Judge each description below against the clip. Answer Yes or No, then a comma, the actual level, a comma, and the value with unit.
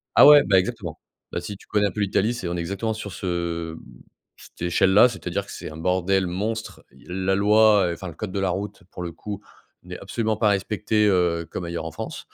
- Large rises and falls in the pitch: No, average, 2.9 semitones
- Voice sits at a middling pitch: No, very low, 95 Hz